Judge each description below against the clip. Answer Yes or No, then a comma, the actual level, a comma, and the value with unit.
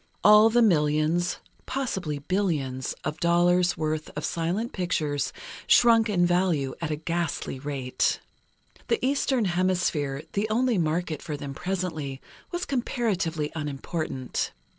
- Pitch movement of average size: Yes, average, 5.0 semitones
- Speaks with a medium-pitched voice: Yes, medium, 170 Hz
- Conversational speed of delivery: No, slow, 120 wpm